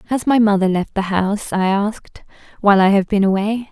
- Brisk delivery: Yes, fast, 210 wpm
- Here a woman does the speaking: Yes, female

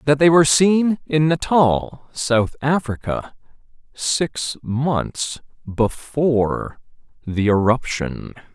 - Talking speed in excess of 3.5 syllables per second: No, 3.1 syllables/s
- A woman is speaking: No, male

